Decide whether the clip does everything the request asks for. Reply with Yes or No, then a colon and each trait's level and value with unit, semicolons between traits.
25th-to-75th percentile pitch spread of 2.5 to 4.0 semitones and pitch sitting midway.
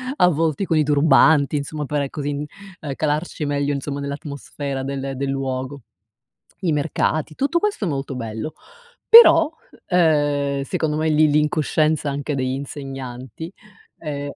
No: narrow, 2.1 semitones; medium, 145 Hz